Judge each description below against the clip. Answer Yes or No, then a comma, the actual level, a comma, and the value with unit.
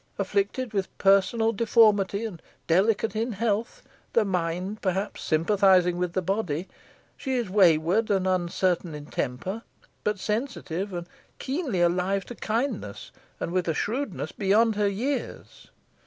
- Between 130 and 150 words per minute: Yes, slow, 135 wpm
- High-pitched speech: Yes, high, 195 Hz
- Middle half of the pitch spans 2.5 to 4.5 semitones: Yes, average, 3.7 semitones